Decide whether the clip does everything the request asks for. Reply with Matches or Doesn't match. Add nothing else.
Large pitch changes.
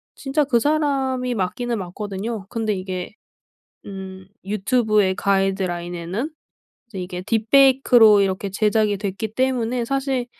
Doesn't match